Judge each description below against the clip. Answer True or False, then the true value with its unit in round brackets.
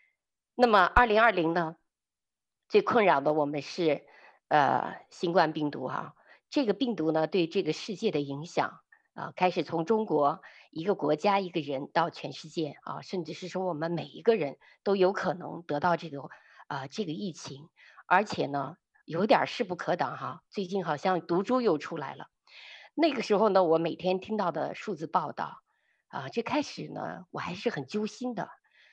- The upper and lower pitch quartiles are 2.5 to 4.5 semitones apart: False (5.2 semitones)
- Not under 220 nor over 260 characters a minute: True (250 characters per minute)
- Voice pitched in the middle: True (180 Hz)